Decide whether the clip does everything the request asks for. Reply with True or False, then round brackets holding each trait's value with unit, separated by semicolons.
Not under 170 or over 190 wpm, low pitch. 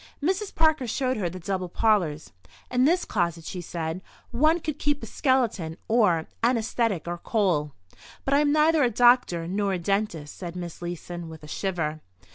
False (175 wpm; 200 Hz)